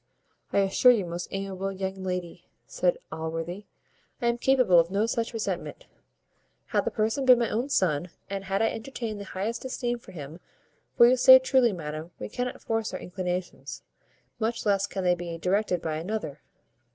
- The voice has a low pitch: No, high, 195 Hz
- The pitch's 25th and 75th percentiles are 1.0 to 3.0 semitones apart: No, average, 4.8 semitones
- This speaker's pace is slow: No, average, 175 wpm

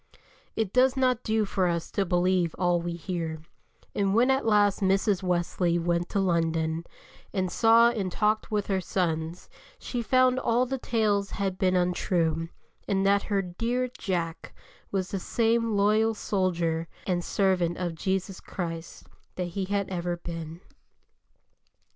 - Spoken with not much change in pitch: No, average, 3.5 semitones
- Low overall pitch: No, high, 190 Hz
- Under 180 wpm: Yes, average, 150 wpm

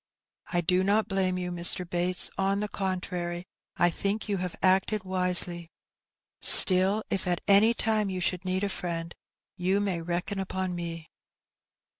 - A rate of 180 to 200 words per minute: No, average, 155 wpm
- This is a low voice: No, medium, 185 Hz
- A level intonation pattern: Yes, narrow, 2.0 semitones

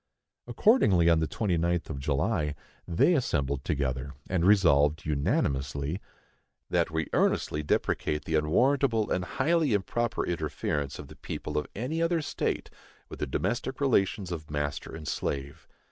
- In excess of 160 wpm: No, average, 140 wpm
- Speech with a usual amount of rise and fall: No, wide, 7.2 semitones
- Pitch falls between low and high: No, very low, 80 Hz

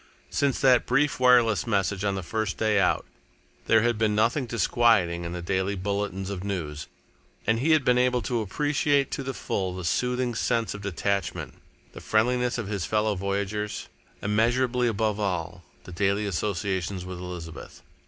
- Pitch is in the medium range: No, low, 105 Hz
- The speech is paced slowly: No, average, 165 wpm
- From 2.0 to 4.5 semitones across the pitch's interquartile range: Yes, average, 4.1 semitones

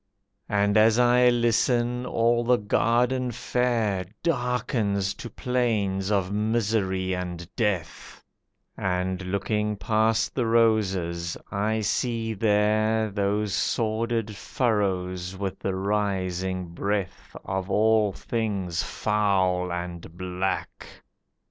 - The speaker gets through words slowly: Yes, slow, 100 wpm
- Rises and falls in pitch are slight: No, average, 3.3 semitones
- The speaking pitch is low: Yes, low, 105 Hz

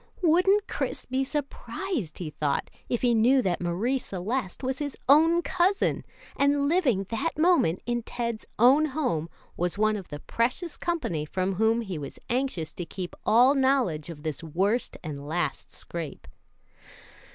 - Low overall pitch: No, high, 235 Hz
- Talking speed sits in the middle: Yes, average, 155 wpm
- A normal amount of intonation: No, wide, 8.2 semitones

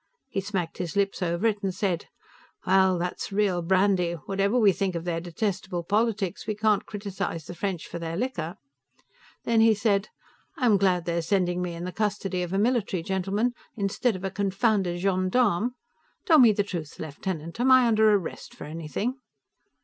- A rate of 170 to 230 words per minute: Yes, average, 175 wpm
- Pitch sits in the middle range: No, high, 195 Hz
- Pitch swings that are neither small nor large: Yes, average, 3.2 semitones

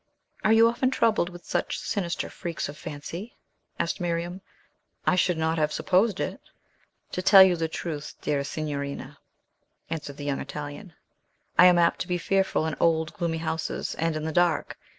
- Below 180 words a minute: Yes, average, 170 wpm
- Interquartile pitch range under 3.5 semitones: Yes, average, 2.9 semitones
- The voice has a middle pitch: Yes, medium, 165 Hz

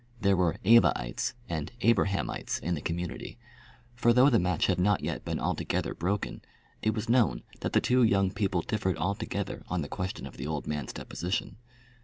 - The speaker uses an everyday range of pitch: Yes, average, 4.2 semitones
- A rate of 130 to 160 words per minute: No, average, 180 wpm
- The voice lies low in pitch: Yes, very low, 95 Hz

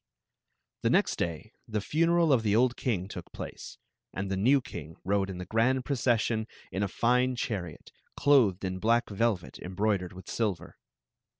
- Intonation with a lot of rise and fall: No, average, 4.6 semitones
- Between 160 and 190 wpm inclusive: Yes, average, 165 wpm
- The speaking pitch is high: No, low, 110 Hz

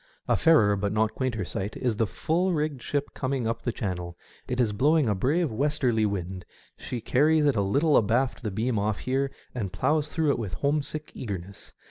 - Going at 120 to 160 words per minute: No, average, 200 wpm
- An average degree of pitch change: No, wide, 6.0 semitones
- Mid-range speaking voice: No, low, 125 Hz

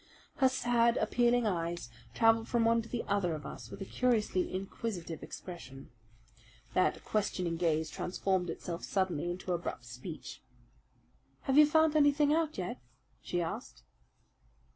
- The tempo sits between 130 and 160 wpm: Yes, average, 140 wpm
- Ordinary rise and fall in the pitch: No, wide, 5.8 semitones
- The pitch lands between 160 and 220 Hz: Yes, high, 190 Hz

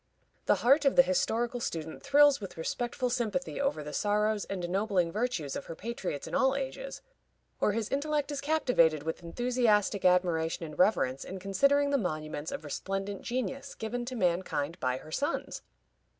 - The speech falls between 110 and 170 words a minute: Yes, average, 165 wpm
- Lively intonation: Yes, wide, 7.3 semitones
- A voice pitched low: No, high, 210 Hz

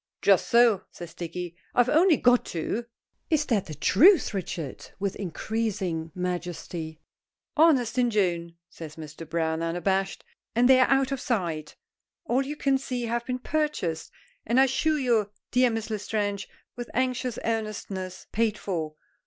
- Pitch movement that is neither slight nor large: No, wide, 6.4 semitones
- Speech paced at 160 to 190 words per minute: No, average, 150 wpm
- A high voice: Yes, high, 215 Hz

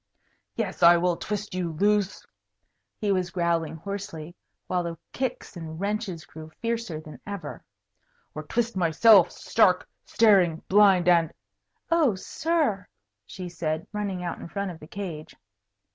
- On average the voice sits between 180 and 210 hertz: Yes, medium, 185 Hz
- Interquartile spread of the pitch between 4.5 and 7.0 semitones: No, average, 3.8 semitones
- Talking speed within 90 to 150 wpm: Yes, average, 145 wpm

